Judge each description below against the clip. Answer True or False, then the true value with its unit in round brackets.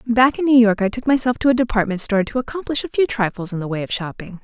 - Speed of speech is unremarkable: False (285 wpm)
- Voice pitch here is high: True (230 Hz)